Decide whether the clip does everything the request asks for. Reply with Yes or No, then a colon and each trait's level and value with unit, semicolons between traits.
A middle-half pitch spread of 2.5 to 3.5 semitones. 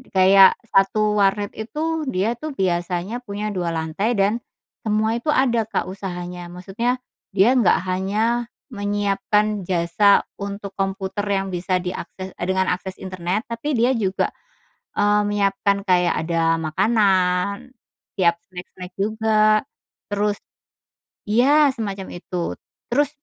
Yes: average, 2.9 semitones